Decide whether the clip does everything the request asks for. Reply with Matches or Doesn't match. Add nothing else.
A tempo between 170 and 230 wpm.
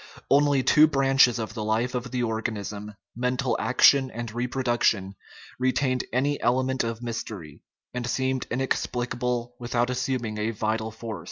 Doesn't match